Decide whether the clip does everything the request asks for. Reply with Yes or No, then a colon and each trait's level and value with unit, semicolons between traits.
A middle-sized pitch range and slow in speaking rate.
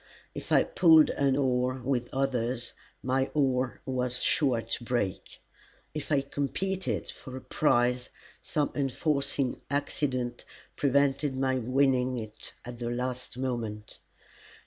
No: narrow, 2.1 semitones; slow, 125 wpm